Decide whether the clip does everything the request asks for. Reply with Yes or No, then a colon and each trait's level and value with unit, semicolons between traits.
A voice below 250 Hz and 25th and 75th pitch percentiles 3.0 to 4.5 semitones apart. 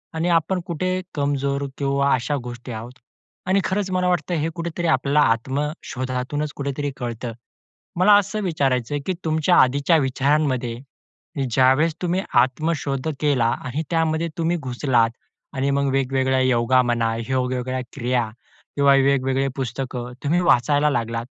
Yes: medium, 140 Hz; average, 3.7 semitones